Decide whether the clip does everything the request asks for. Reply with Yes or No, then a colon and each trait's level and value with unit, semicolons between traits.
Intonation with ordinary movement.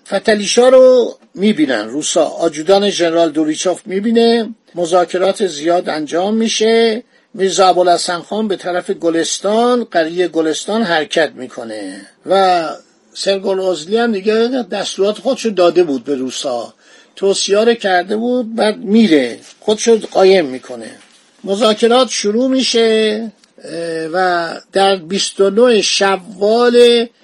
Yes: average, 4.4 semitones